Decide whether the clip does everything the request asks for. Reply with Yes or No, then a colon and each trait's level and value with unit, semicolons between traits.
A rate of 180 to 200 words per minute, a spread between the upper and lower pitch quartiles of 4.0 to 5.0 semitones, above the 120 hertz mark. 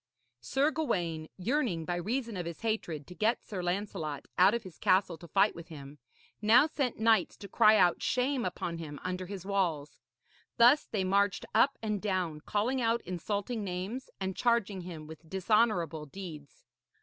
No: average, 170 wpm; average, 4.7 semitones; high, 190 Hz